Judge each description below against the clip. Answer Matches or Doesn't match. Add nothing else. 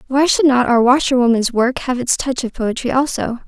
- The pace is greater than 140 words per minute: Matches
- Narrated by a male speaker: Doesn't match